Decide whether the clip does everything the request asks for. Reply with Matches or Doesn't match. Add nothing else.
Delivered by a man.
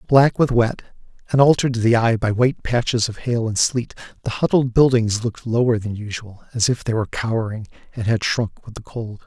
Matches